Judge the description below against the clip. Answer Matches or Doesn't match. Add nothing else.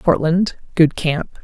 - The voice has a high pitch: Doesn't match